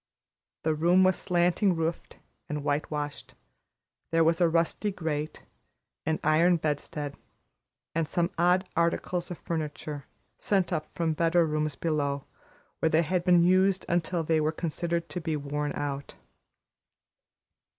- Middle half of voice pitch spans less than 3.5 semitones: Yes, narrow, 2.4 semitones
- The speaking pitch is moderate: Yes, medium, 165 Hz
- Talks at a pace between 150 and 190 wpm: No, slow, 135 wpm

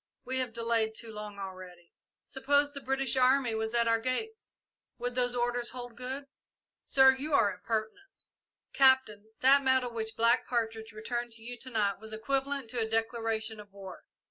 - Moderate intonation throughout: Yes, average, 3.0 semitones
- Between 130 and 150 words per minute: No, average, 170 wpm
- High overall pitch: Yes, high, 235 Hz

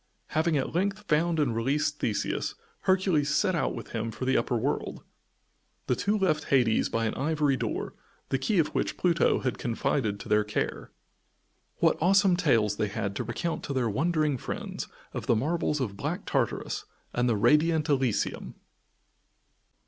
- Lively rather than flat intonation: Yes, wide, 6.1 semitones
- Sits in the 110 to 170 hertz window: Yes, medium, 140 Hz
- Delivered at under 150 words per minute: No, average, 165 wpm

